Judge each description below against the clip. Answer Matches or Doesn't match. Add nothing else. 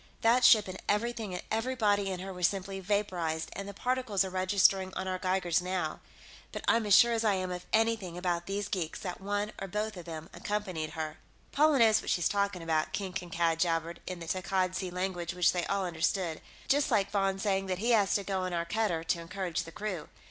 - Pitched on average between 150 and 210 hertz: Matches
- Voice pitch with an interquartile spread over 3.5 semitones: Doesn't match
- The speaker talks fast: Matches